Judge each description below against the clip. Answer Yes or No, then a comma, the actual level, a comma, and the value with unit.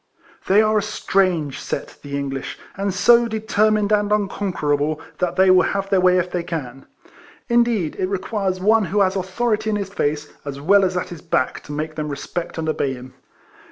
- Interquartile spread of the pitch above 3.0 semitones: Yes, average, 5.1 semitones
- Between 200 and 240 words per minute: Yes, fast, 205 wpm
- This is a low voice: No, medium, 185 Hz